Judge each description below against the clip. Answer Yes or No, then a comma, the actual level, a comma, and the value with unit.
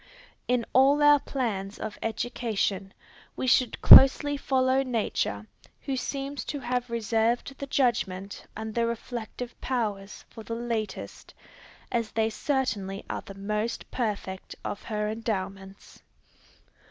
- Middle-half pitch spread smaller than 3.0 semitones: No, average, 3.6 semitones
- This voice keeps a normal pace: No, slow, 125 wpm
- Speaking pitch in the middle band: No, high, 230 Hz